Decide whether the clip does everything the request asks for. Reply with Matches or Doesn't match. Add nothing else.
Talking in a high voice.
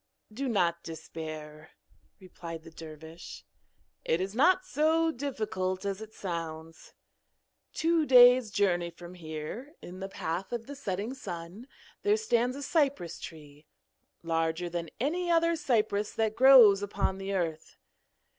Matches